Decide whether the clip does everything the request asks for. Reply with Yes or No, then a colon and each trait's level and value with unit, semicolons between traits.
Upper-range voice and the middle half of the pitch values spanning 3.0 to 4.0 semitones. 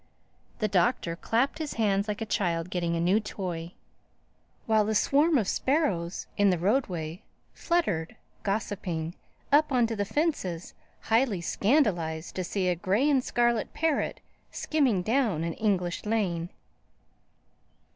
No: high, 205 Hz; wide, 5.5 semitones